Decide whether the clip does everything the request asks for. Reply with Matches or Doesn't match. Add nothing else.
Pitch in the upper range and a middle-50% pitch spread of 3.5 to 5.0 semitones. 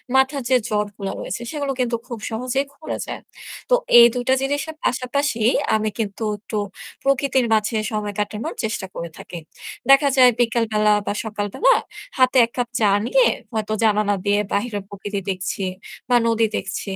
Matches